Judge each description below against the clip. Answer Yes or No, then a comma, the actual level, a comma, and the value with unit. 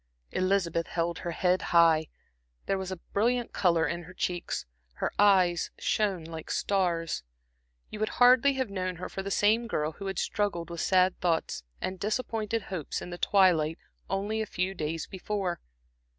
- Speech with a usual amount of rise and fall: Yes, average, 3.2 semitones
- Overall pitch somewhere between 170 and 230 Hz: Yes, medium, 185 Hz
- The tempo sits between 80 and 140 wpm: No, average, 165 wpm